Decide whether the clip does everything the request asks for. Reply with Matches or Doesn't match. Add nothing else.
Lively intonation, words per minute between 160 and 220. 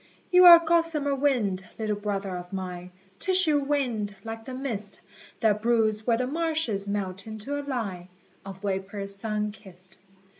Doesn't match